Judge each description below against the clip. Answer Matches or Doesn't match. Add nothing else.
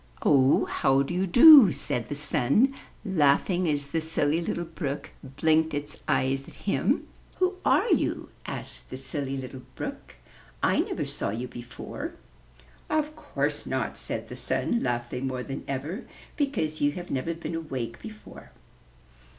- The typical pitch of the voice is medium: Matches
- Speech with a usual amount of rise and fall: Matches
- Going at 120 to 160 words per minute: Matches